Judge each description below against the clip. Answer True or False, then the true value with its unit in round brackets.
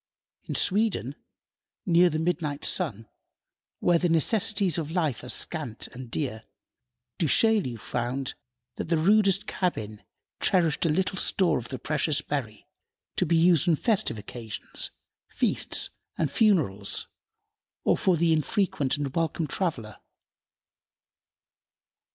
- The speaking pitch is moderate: True (160 Hz)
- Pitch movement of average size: False (5.8 semitones)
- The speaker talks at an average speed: False (125 wpm)